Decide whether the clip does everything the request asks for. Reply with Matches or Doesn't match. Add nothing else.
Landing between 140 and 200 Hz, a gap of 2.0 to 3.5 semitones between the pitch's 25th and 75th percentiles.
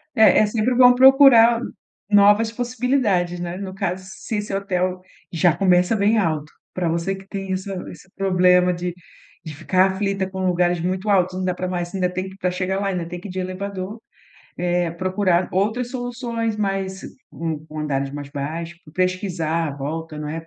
Matches